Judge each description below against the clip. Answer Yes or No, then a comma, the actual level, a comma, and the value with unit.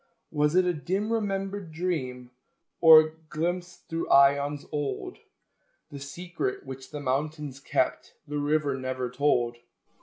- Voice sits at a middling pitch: Yes, medium, 150 Hz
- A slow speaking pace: Yes, slow, 125 wpm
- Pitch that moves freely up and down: No, average, 4.0 semitones